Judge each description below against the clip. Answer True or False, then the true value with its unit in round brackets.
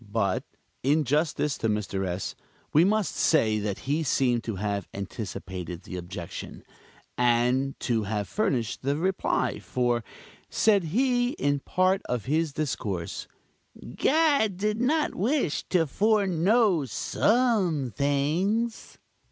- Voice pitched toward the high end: False (145 Hz)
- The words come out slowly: True (125 wpm)